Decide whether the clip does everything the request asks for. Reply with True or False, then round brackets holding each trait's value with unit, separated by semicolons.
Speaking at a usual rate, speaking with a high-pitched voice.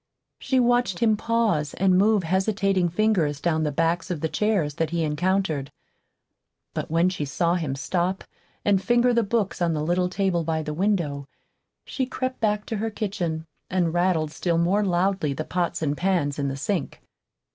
False (180 wpm; 180 Hz)